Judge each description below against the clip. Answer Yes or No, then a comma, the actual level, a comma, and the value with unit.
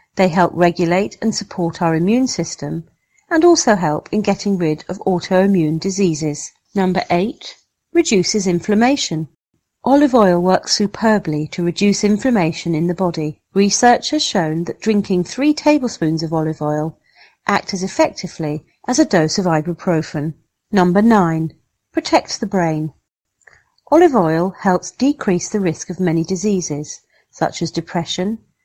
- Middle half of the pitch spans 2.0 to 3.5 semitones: No, average, 4.6 semitones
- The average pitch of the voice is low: No, medium, 185 Hz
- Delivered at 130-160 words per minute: Yes, average, 140 wpm